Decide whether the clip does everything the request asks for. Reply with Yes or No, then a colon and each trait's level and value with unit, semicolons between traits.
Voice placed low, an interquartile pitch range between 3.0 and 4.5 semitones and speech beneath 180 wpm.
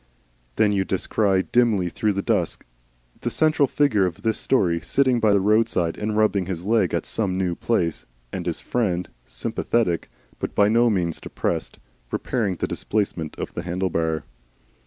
Yes: low, 100 Hz; average, 3.8 semitones; average, 165 wpm